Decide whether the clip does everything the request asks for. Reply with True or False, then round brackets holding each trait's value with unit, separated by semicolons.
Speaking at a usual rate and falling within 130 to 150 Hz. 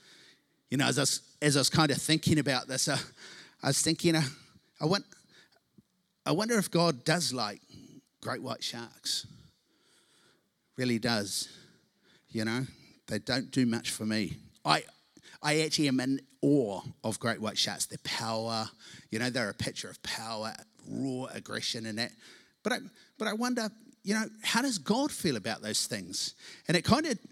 True (175 wpm; 140 Hz)